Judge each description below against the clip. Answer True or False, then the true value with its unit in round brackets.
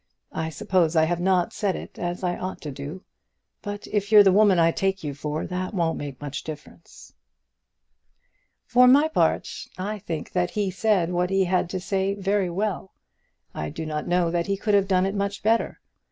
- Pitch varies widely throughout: False (3.1 semitones)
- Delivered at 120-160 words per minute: False (195 wpm)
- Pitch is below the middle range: False (185 Hz)